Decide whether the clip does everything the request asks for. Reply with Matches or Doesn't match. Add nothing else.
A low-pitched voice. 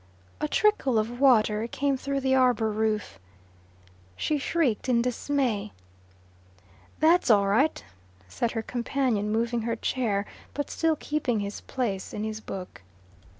Doesn't match